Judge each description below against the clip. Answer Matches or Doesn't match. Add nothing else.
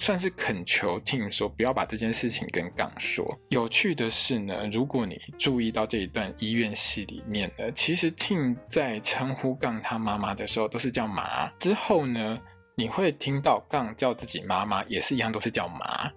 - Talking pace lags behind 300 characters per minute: Matches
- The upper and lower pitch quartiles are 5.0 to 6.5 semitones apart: Doesn't match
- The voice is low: Matches